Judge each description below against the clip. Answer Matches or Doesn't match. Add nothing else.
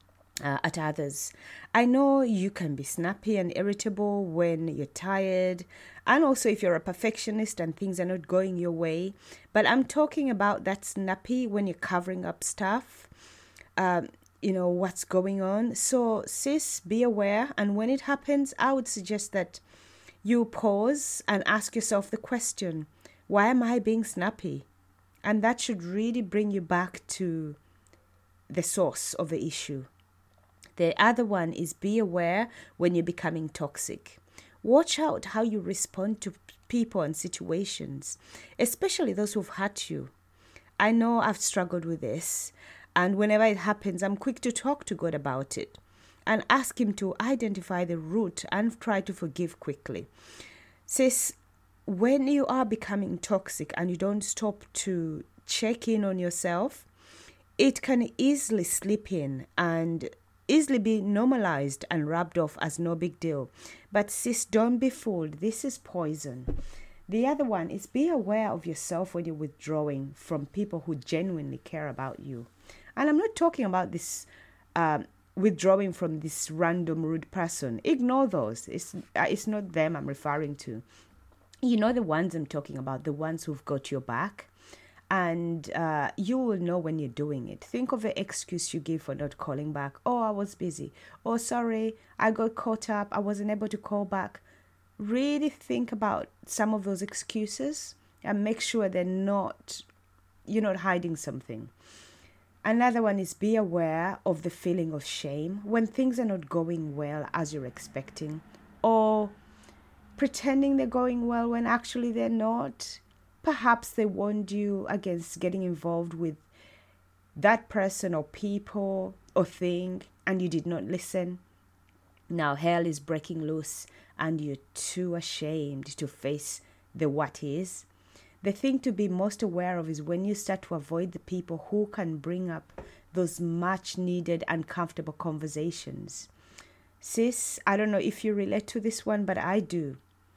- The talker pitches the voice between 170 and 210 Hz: Matches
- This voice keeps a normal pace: Matches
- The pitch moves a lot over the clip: Matches